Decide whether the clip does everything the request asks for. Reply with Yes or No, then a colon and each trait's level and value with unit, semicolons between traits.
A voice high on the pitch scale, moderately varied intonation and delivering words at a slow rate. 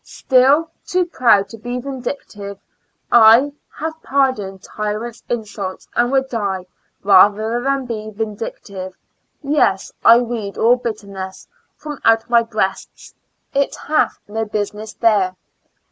Yes: high, 225 Hz; average, 4.0 semitones; slow, 125 wpm